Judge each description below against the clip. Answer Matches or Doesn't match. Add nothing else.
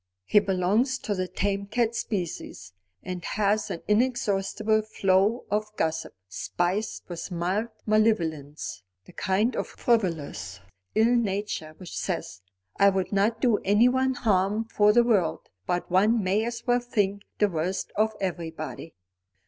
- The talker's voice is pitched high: Matches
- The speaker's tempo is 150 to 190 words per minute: Doesn't match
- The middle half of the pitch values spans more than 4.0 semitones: Doesn't match